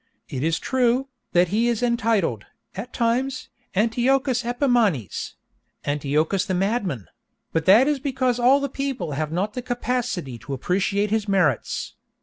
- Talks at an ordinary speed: No, slow, 130 wpm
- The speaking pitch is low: No, high, 220 Hz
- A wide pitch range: Yes, wide, 6.3 semitones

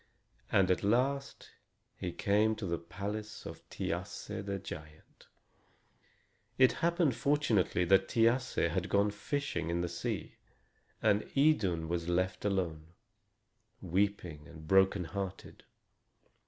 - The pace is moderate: No, slow, 115 wpm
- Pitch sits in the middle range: No, very low, 95 Hz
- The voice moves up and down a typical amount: Yes, average, 4.1 semitones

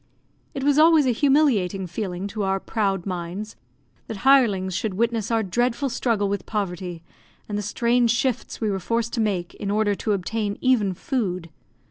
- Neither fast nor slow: Yes, average, 170 wpm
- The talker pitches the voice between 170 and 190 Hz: No, high, 210 Hz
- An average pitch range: Yes, average, 3.7 semitones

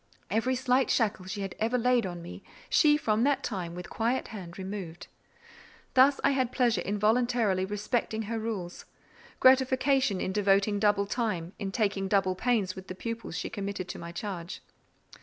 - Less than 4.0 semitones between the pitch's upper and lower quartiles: No, average, 4.3 semitones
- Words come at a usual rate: Yes, average, 170 wpm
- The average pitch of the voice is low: No, high, 210 Hz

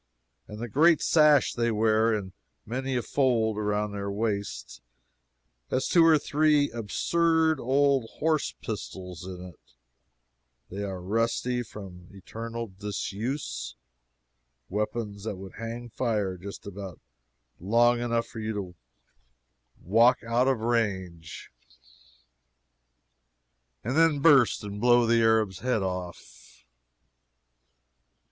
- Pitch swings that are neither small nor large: Yes, average, 3.9 semitones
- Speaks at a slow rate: Yes, slow, 115 wpm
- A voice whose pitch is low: Yes, low, 115 Hz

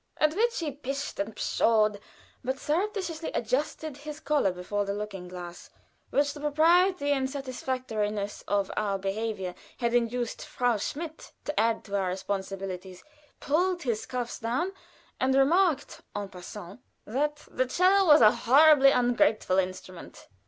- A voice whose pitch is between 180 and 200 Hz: No, high, 245 Hz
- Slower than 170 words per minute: Yes, average, 140 wpm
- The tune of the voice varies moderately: No, wide, 6.6 semitones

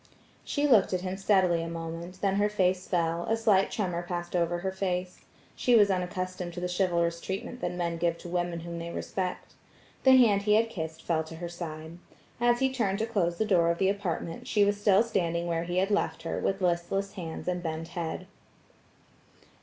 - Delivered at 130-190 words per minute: No, fast, 205 wpm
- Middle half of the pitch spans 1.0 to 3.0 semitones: Yes, average, 2.7 semitones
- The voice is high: No, medium, 180 Hz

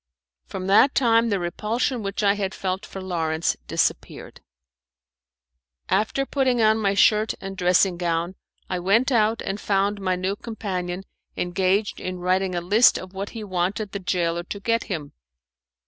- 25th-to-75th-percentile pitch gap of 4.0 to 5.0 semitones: No, average, 2.9 semitones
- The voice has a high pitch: Yes, high, 195 Hz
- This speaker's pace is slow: No, average, 160 wpm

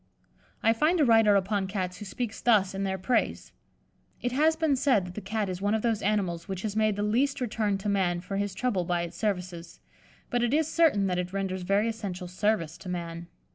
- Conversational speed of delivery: No, fast, 220 wpm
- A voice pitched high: Yes, high, 200 Hz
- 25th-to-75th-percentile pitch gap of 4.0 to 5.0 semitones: No, average, 3.5 semitones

